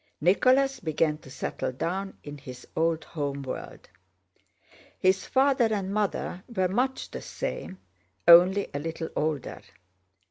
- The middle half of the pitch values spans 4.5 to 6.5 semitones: Yes, wide, 5.4 semitones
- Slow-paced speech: Yes, slow, 130 wpm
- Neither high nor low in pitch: Yes, medium, 180 Hz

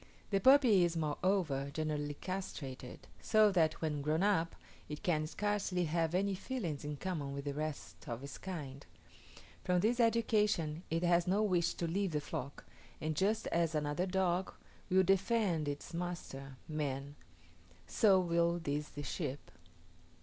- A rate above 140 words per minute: Yes, average, 150 wpm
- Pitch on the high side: No, medium, 170 Hz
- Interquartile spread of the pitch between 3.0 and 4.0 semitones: No, average, 4.4 semitones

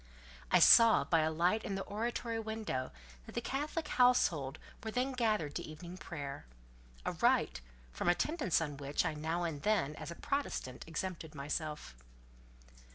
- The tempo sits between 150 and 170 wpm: Yes, average, 155 wpm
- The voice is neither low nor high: Yes, medium, 170 Hz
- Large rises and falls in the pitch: Yes, wide, 7.2 semitones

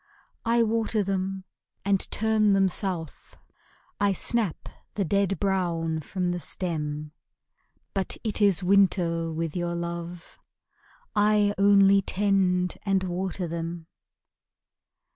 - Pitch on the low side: No, high, 190 Hz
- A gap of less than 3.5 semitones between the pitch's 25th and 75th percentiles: Yes, average, 2.7 semitones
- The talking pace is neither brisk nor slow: No, slow, 110 wpm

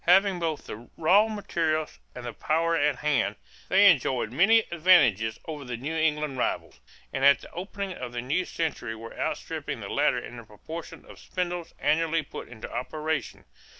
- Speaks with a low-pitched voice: No, medium, 155 Hz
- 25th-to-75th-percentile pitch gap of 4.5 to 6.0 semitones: Yes, wide, 5.5 semitones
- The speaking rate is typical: Yes, average, 175 wpm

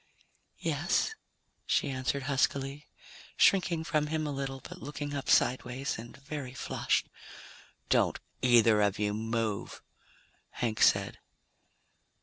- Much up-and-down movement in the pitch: No, average, 3.8 semitones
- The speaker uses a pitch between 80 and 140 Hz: Yes, low, 135 Hz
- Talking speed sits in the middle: No, slow, 115 wpm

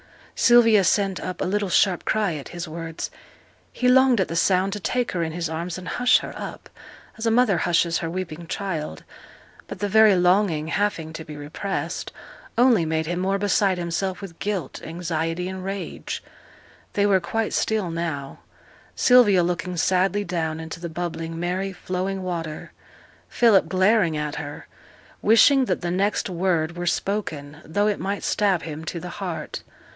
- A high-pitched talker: No, medium, 180 Hz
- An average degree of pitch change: Yes, average, 3.5 semitones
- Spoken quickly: No, average, 170 wpm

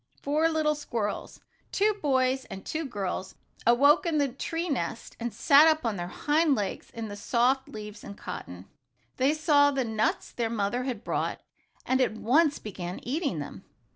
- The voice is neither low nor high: No, very high, 255 Hz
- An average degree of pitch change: No, wide, 5.8 semitones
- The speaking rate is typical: Yes, average, 170 wpm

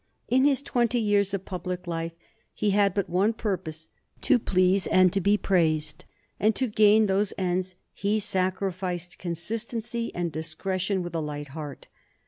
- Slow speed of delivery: No, average, 155 wpm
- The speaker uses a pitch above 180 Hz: Yes, high, 190 Hz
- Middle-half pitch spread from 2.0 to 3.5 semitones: Yes, average, 3.2 semitones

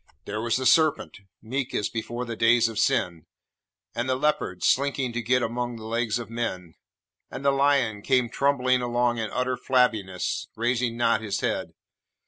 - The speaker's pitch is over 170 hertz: No, low, 120 Hz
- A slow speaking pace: No, average, 170 wpm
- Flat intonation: Yes, narrow, 2.3 semitones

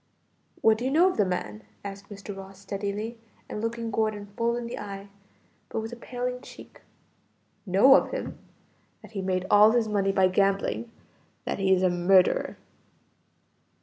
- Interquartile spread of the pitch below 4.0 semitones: Yes, average, 3.1 semitones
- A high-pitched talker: Yes, high, 205 Hz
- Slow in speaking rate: No, average, 170 wpm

